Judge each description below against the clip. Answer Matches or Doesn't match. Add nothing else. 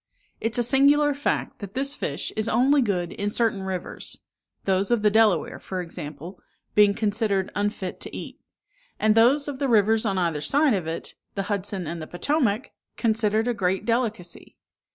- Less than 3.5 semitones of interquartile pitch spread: Doesn't match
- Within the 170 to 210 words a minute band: Matches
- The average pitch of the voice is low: Doesn't match